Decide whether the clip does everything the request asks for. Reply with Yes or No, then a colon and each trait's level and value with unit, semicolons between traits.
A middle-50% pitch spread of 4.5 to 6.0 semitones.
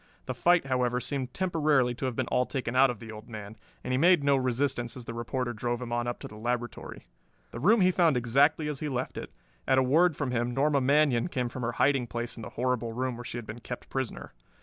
No: average, 2.9 semitones